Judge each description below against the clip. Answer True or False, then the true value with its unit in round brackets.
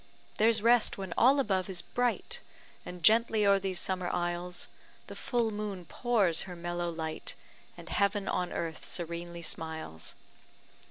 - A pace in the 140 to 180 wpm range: True (145 wpm)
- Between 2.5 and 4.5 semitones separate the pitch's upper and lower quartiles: True (3.9 semitones)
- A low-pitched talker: False (185 Hz)